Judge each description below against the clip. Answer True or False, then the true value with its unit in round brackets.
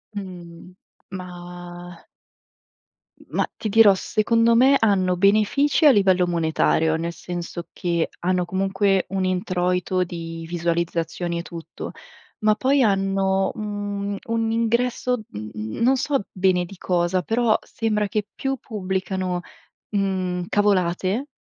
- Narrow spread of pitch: False (3.3 semitones)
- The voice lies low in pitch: False (190 Hz)